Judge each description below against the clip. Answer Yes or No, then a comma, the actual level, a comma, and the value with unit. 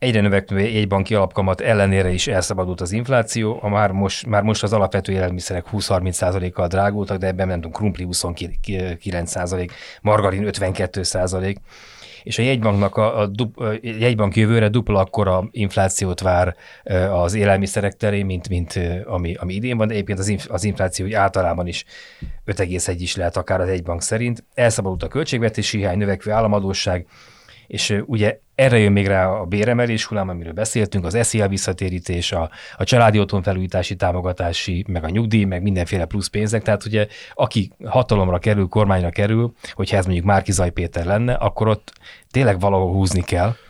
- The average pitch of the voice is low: Yes, low, 100 Hz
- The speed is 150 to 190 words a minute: Yes, fast, 155 wpm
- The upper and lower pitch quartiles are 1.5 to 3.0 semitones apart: Yes, narrow, 2.6 semitones